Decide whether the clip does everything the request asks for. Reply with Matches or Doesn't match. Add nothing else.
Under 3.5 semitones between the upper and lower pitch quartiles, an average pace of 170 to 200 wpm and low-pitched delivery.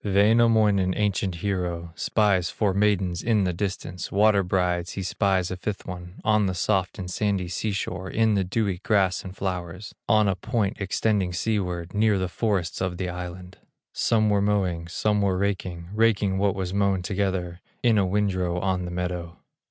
Matches